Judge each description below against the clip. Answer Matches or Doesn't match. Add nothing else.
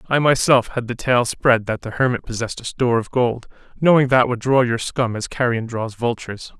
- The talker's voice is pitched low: Matches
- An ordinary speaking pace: Doesn't match